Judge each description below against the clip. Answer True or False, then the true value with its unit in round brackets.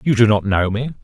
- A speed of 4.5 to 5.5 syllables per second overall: False (6.0 syllables/s)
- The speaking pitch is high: False (110 Hz)